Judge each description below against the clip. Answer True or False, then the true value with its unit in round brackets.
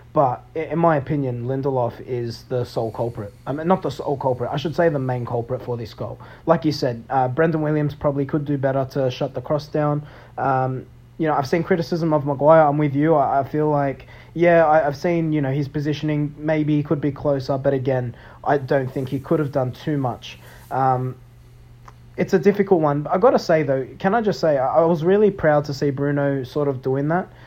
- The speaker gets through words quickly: True (225 wpm)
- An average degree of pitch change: True (3.4 semitones)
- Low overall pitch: False (145 Hz)